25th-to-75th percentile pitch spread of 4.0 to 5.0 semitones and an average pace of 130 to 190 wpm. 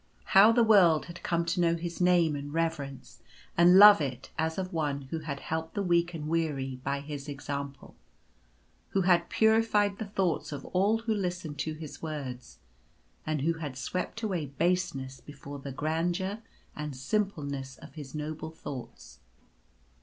Yes: average, 4.3 semitones; average, 160 wpm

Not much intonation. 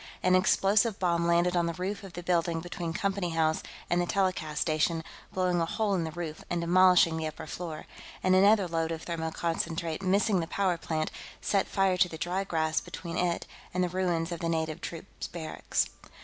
Yes: narrow, 2.1 semitones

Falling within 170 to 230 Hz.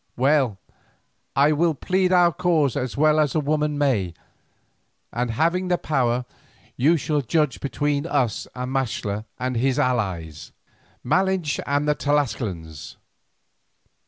No: medium, 140 Hz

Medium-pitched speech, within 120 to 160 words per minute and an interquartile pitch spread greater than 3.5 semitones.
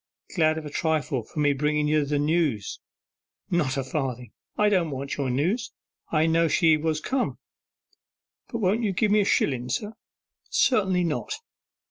Yes: medium, 155 Hz; average, 155 wpm; average, 4.5 semitones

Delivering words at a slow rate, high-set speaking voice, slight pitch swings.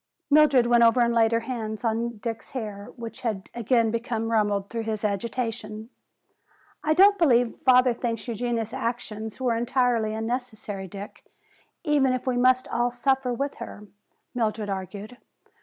No: average, 150 wpm; high, 235 Hz; narrow, 2.3 semitones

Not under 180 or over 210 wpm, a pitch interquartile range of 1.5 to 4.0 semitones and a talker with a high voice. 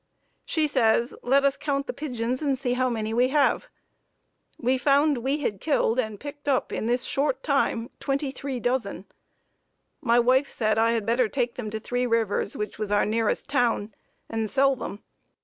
Yes: average, 185 wpm; average, 3.4 semitones; very high, 250 Hz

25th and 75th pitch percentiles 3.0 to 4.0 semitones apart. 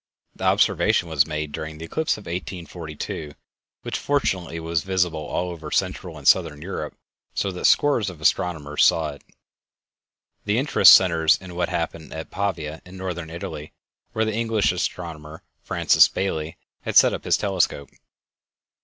Yes: average, 3.3 semitones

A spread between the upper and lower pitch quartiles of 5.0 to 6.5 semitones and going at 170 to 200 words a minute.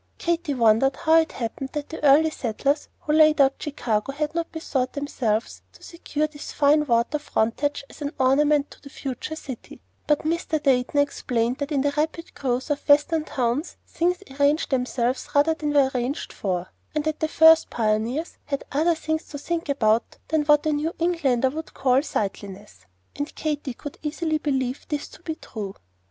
No: average, 3.5 semitones; average, 180 wpm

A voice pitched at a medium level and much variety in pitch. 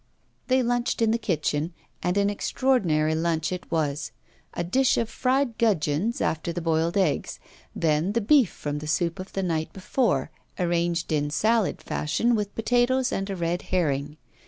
Yes: medium, 180 Hz; wide, 6.3 semitones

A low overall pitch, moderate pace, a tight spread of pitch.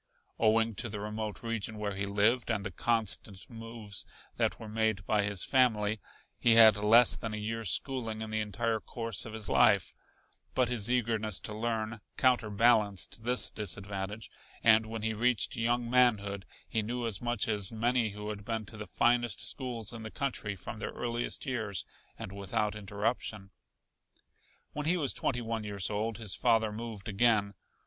Yes: low, 110 Hz; average, 170 wpm; narrow, 2.1 semitones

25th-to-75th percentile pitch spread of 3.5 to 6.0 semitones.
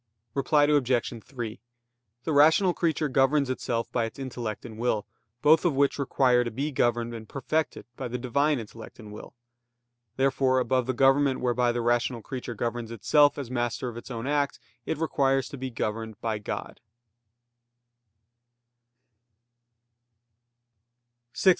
No: average, 3.1 semitones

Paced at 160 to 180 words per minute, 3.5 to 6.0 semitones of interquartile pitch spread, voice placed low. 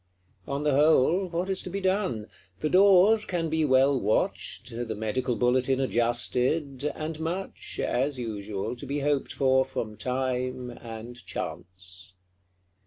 No: slow, 135 wpm; average, 4.8 semitones; low, 130 Hz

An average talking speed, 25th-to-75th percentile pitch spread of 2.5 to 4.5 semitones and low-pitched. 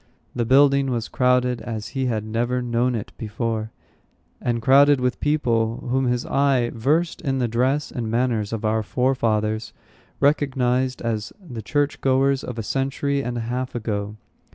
Yes: average, 160 wpm; average, 2.9 semitones; low, 125 Hz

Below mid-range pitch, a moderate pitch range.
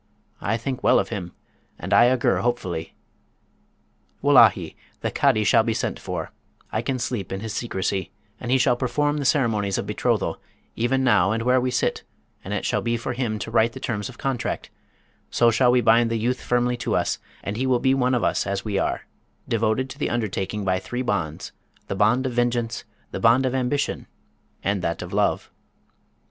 Yes: low, 120 Hz; average, 3.2 semitones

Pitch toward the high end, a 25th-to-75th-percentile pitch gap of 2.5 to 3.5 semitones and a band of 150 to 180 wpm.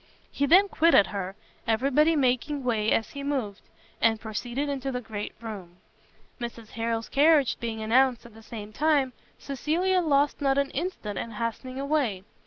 No: very high, 255 Hz; average, 4.2 semitones; average, 165 wpm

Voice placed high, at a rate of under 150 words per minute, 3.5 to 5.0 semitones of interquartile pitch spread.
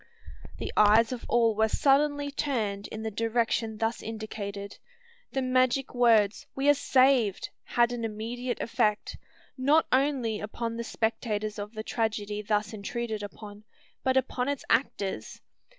No: high, 230 Hz; average, 140 wpm; average, 3.1 semitones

